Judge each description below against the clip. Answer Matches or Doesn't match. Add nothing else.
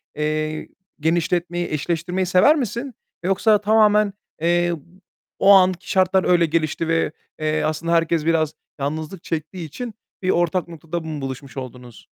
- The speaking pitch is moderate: Matches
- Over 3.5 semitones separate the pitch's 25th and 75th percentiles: Doesn't match